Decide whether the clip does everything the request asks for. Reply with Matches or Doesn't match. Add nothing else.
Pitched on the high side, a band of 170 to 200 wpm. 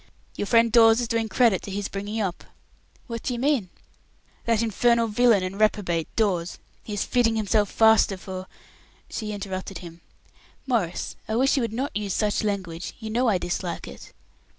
Matches